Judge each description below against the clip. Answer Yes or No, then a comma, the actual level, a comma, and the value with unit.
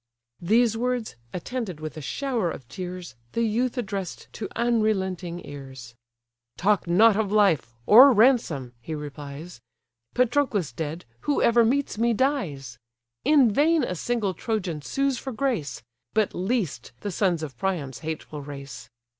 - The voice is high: Yes, high, 195 Hz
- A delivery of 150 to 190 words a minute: No, average, 140 wpm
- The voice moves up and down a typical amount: No, wide, 7.4 semitones